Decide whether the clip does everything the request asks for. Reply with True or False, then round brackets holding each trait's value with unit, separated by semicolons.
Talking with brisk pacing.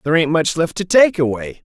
True (245 wpm)